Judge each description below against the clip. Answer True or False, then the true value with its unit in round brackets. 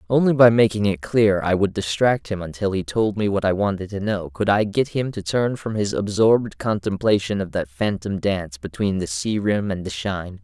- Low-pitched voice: True (100 Hz)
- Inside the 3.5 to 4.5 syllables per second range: False (5.2 syllables/s)